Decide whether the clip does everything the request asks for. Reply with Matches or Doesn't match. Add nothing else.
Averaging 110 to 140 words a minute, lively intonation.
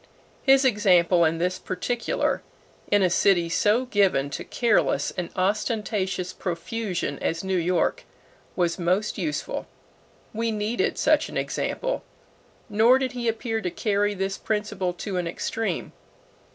Doesn't match